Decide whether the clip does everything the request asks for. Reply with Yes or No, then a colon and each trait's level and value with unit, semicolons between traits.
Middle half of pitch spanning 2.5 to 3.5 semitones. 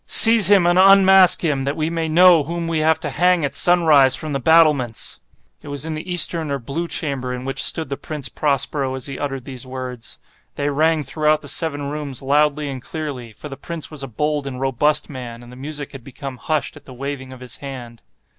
Yes: average, 3.2 semitones